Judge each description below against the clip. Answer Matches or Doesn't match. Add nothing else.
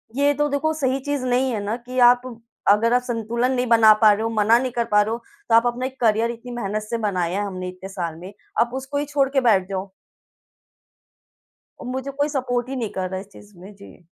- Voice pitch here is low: Doesn't match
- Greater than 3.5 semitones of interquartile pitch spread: Matches